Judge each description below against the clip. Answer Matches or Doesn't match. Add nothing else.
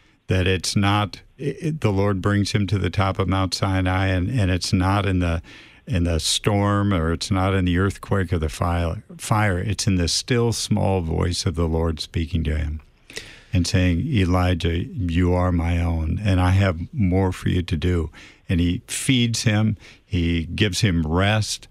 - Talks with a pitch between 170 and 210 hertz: Doesn't match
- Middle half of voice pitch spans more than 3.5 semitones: Doesn't match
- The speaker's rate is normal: Matches